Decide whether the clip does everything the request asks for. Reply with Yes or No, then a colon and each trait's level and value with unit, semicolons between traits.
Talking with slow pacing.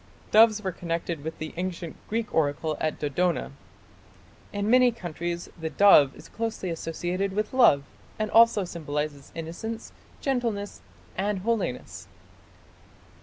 Yes: slow, 120 wpm